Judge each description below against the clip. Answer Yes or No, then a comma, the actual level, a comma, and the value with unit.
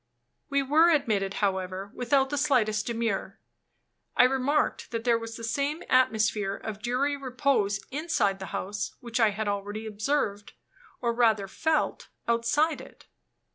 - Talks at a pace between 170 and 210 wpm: No, average, 140 wpm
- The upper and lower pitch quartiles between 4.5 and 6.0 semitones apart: Yes, average, 5.1 semitones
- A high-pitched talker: Yes, high, 230 Hz